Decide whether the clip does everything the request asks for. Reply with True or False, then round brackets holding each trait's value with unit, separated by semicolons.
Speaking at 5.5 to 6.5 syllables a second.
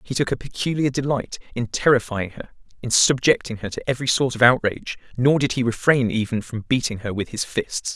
True (5.7 syllables/s)